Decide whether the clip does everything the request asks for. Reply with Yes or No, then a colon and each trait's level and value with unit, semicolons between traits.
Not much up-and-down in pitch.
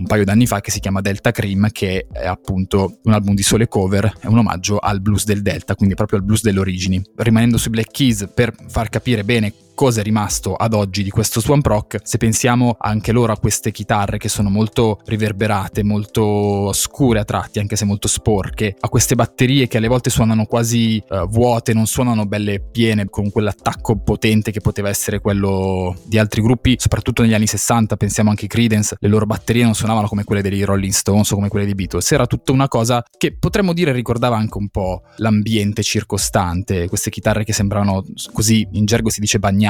Yes: narrow, 2.2 semitones